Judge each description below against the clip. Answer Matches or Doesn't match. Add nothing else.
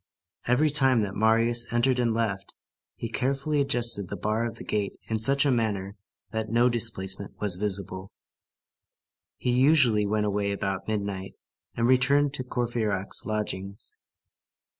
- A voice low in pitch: Matches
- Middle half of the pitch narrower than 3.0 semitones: Doesn't match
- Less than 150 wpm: Matches